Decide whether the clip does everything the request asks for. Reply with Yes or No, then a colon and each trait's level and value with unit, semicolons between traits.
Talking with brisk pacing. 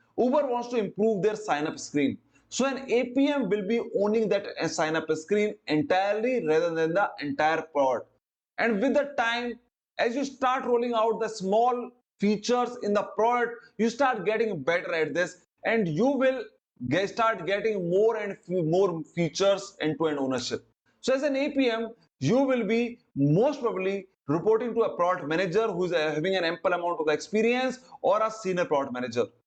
No: average, 170 wpm